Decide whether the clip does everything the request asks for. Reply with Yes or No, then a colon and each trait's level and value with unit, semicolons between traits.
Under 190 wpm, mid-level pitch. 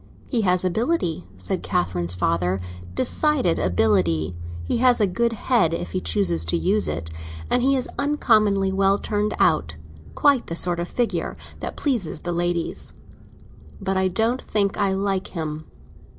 Yes: average, 160 wpm; medium, 180 Hz